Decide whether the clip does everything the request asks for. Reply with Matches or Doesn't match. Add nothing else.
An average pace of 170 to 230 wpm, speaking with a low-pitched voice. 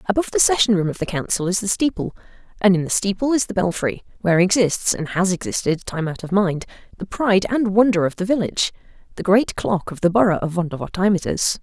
Doesn't match